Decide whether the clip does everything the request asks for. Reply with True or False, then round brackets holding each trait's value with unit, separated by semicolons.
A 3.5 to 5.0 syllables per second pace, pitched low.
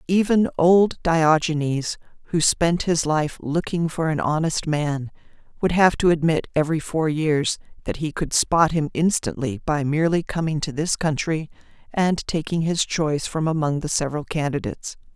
False (4.8 syllables/s; 160 Hz)